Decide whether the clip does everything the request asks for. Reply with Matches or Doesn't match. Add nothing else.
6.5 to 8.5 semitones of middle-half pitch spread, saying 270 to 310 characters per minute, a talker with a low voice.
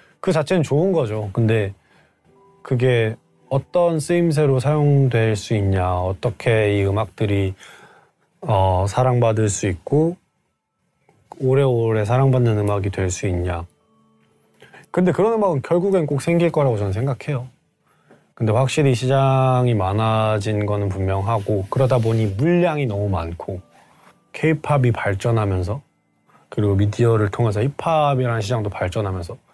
Doesn't match